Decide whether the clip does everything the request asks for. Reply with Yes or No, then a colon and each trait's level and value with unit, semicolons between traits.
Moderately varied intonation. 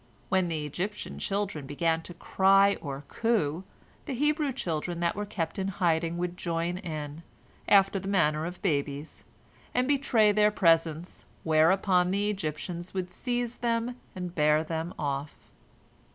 Yes: average, 4.1 semitones